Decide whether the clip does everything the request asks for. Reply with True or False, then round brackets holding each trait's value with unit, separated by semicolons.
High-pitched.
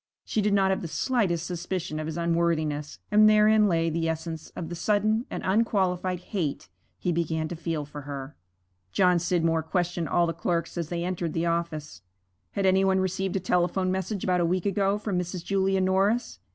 False (175 Hz)